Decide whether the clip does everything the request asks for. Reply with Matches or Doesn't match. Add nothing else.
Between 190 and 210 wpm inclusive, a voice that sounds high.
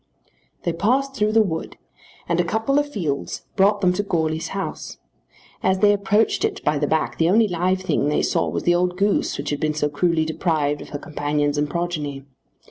Doesn't match